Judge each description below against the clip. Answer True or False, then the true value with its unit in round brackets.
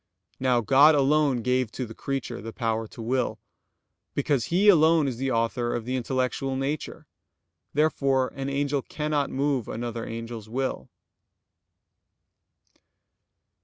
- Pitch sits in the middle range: False (130 Hz)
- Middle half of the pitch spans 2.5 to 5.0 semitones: True (3.2 semitones)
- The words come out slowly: True (130 wpm)